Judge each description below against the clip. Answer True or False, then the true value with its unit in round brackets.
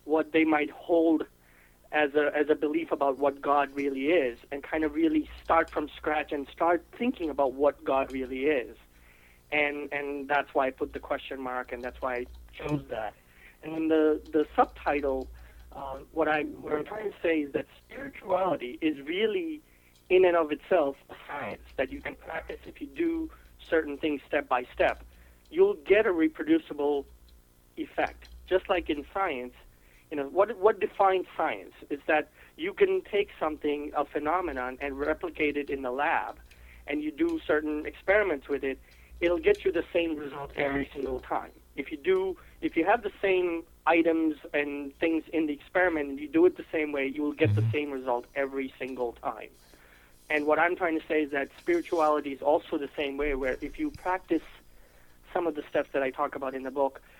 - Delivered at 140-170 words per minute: False (195 wpm)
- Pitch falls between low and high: True (150 Hz)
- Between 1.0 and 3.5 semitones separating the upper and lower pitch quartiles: False (4.3 semitones)